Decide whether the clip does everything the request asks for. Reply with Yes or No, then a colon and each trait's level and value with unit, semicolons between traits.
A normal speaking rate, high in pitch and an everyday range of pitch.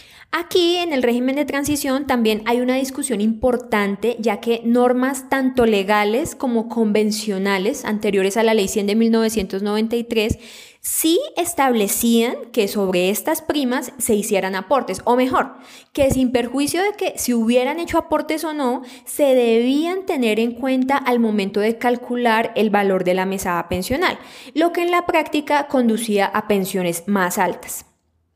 Yes: average, 150 wpm; high, 235 Hz; average, 4.3 semitones